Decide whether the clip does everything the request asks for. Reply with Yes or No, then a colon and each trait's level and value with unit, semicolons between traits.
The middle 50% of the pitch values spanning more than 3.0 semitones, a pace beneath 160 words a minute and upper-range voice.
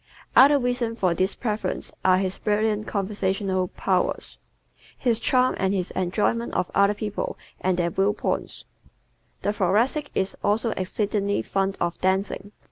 No: average, 2.7 semitones; average, 140 wpm; high, 200 Hz